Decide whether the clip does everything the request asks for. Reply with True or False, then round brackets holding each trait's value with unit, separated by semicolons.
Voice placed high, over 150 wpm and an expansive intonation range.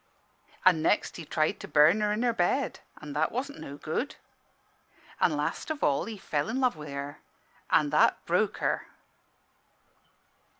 False (165 Hz; 165 wpm; 7.2 semitones)